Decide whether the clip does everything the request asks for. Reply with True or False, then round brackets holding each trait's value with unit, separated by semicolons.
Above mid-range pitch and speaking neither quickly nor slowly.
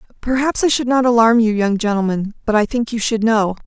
False (225 Hz; 230 wpm)